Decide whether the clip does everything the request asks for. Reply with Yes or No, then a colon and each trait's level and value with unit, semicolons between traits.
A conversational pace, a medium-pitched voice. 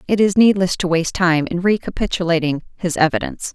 Yes: average, 170 wpm; medium, 180 Hz